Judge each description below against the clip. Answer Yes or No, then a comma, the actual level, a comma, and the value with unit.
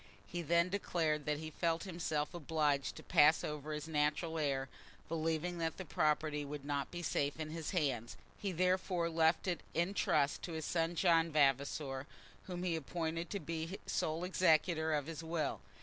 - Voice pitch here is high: No, medium, 160 Hz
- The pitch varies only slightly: Yes, narrow, 2.3 semitones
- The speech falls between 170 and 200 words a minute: Yes, average, 175 wpm